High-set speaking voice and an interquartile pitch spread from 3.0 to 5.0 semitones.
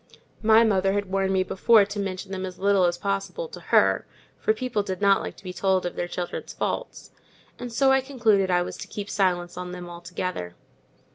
No: high, 195 Hz; narrow, 2.5 semitones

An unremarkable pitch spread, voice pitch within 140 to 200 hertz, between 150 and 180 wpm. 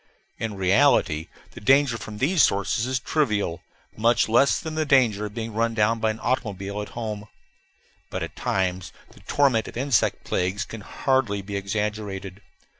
No: average, 3.9 semitones; low, 110 Hz; average, 165 wpm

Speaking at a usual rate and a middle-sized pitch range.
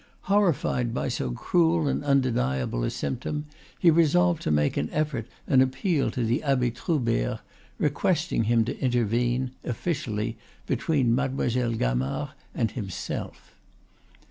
No: slow, 125 wpm; average, 4.8 semitones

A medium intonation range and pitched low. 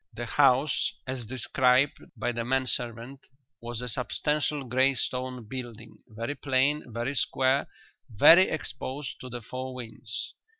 No: narrow, 2.1 semitones; low, 130 Hz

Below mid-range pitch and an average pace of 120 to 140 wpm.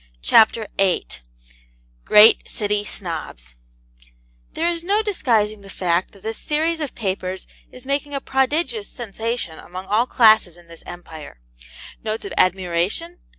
No: high, 215 Hz; slow, 135 wpm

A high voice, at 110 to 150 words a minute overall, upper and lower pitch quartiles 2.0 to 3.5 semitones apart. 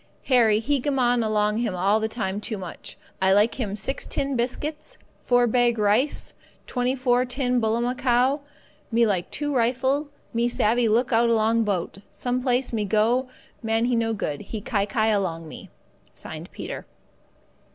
No: high, 235 Hz; average, 160 wpm; average, 2.9 semitones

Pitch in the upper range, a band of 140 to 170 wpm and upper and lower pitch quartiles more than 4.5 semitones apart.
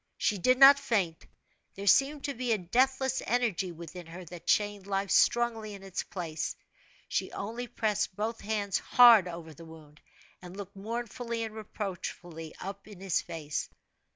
Yes: high, 200 Hz; average, 160 wpm; average, 4.9 semitones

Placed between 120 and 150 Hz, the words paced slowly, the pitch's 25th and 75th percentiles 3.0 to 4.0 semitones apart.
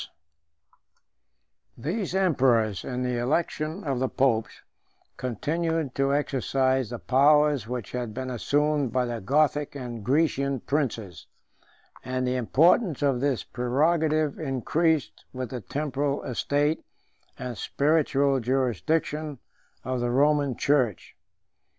Yes: low, 135 Hz; slow, 115 wpm; average, 3.3 semitones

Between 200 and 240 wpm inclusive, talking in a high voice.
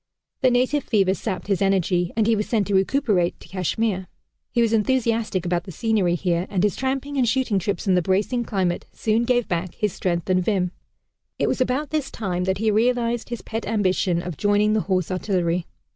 Yes: fast, 205 wpm; high, 205 Hz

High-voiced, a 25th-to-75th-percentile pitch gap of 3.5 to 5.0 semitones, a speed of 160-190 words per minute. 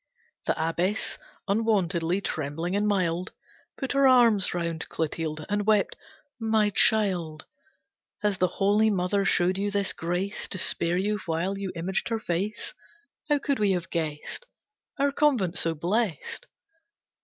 No: high, 195 Hz; average, 3.8 semitones; average, 140 wpm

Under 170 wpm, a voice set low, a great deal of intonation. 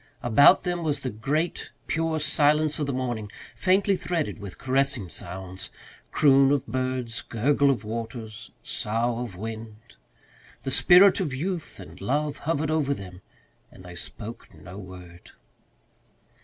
Yes: average, 140 wpm; low, 130 Hz; wide, 5.7 semitones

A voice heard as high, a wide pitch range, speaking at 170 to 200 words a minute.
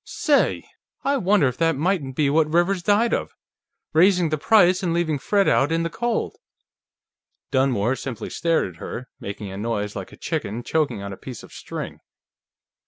No: medium, 160 Hz; wide, 6.4 semitones; average, 175 wpm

